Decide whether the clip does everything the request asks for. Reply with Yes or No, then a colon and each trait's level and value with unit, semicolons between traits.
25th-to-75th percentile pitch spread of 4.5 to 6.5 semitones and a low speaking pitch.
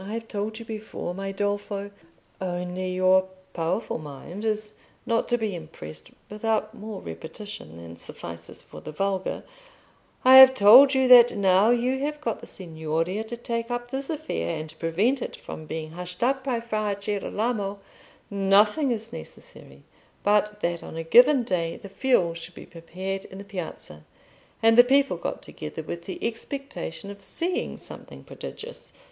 No: average, 5.0 semitones; high, 205 Hz